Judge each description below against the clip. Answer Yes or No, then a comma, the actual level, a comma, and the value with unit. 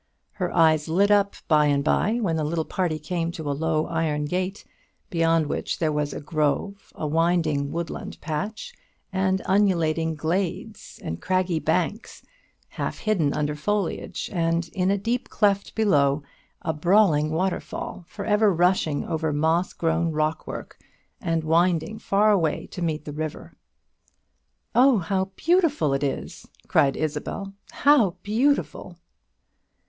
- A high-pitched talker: No, medium, 170 Hz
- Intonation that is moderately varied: Yes, average, 4.2 semitones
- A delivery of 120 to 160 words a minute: Yes, average, 140 wpm